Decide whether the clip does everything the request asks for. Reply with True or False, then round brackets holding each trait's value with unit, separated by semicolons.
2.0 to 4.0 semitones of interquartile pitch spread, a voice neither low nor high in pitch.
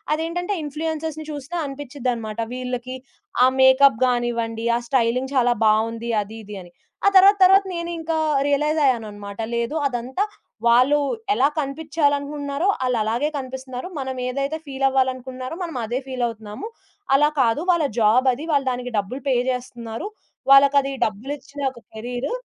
False (3.3 semitones; 260 Hz)